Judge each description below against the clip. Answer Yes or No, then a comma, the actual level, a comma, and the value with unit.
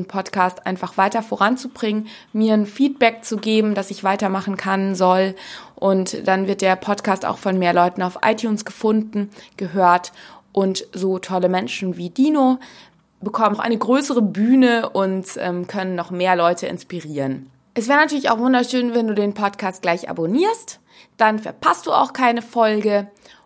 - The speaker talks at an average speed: Yes, average, 155 wpm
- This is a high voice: Yes, high, 200 Hz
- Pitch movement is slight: No, average, 3.6 semitones